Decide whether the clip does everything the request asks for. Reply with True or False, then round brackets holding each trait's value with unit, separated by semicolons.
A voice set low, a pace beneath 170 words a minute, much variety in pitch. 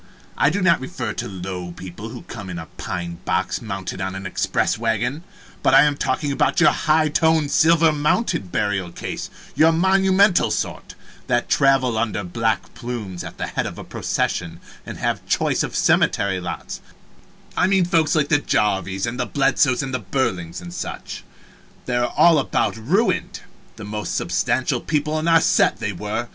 False (120 Hz; 175 wpm; 8.3 semitones)